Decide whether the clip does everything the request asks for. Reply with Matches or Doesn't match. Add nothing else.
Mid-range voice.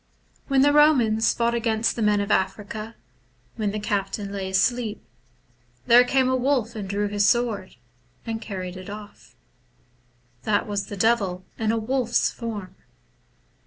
Doesn't match